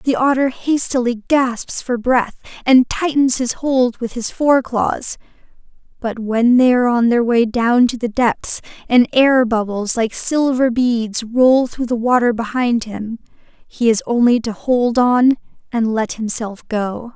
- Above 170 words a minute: No, average, 165 wpm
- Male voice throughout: No, female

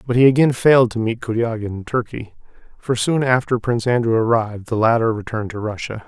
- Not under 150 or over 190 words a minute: No, average, 200 wpm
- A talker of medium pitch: No, low, 115 Hz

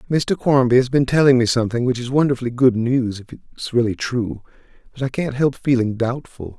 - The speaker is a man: Yes, male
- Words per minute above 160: Yes, average, 200 wpm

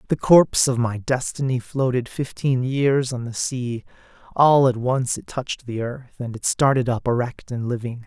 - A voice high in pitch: No, low, 125 Hz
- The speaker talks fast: No, average, 185 wpm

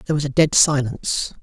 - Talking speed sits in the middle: No, fast, 210 wpm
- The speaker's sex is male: Yes, male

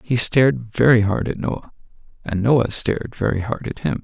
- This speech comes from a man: Yes, male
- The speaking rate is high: No, average, 195 wpm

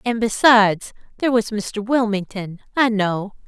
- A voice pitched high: Yes, high, 215 Hz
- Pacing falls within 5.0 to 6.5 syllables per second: No, 4.6 syllables/s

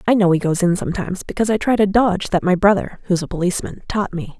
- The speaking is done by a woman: Yes, female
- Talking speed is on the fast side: Yes, fast, 230 wpm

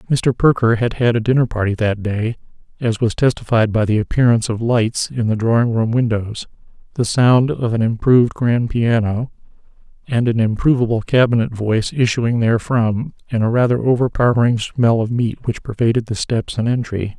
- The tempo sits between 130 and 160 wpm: No, average, 170 wpm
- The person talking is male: Yes, male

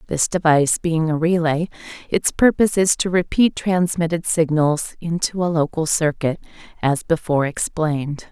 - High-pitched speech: No, medium, 165 Hz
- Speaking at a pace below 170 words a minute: Yes, slow, 135 wpm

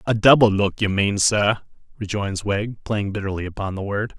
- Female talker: No, male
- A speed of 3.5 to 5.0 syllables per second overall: Yes, 4.9 syllables/s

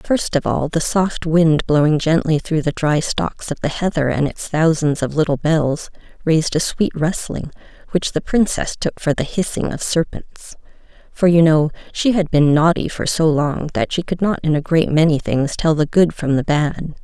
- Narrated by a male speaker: No, female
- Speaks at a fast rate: Yes, fast, 210 wpm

